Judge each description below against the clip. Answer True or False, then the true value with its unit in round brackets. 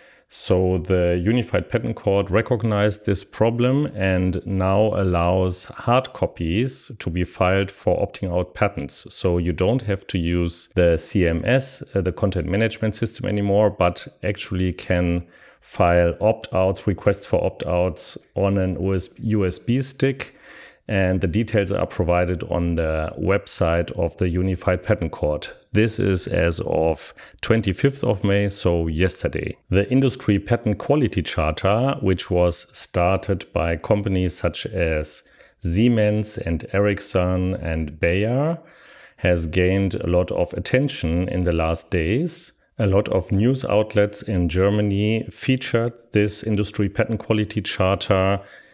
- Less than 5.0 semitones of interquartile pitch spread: True (3.6 semitones)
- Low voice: True (95 Hz)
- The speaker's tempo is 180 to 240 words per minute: False (135 wpm)